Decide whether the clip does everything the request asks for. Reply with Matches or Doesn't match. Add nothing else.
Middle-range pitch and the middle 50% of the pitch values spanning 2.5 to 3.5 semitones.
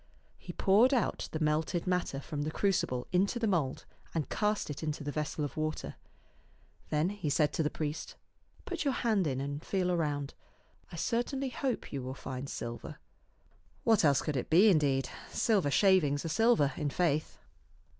Doesn't match